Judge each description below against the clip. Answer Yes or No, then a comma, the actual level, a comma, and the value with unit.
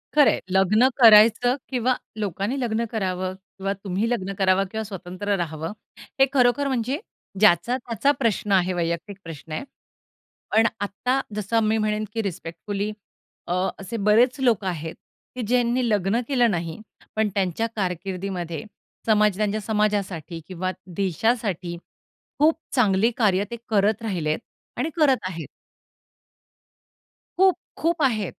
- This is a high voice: Yes, high, 210 Hz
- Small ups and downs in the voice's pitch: No, average, 4.0 semitones